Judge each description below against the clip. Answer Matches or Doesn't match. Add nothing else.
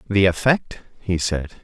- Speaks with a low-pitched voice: Matches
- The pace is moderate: Matches